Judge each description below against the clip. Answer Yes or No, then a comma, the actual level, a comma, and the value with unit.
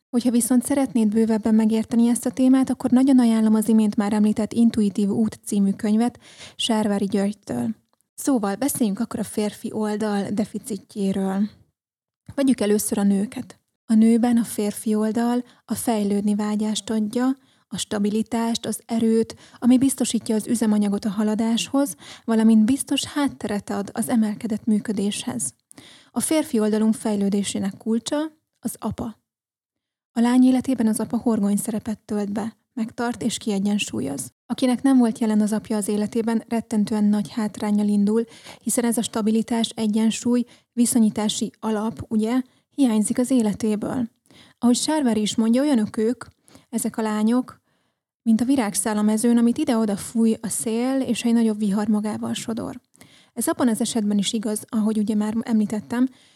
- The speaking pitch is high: Yes, high, 225 Hz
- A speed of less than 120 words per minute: No, average, 145 wpm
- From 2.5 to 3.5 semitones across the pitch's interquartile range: No, narrow, 2.1 semitones